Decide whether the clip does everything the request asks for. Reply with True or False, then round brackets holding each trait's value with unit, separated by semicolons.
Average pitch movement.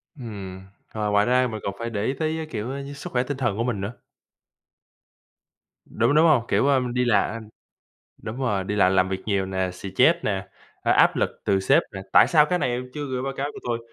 True (4.9 semitones)